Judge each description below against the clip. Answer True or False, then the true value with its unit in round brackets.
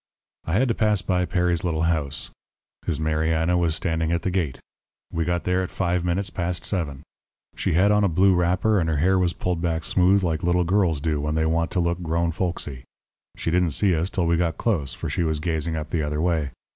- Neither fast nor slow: False (225 wpm)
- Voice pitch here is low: True (85 Hz)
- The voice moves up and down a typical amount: False (2.2 semitones)